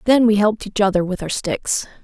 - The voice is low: No, high, 205 Hz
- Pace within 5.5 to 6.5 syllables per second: Yes, 5.7 syllables/s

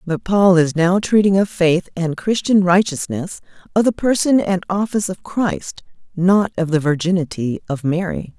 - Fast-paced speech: No, average, 165 wpm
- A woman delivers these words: Yes, female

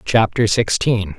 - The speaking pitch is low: Yes, low, 105 Hz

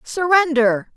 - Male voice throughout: No, female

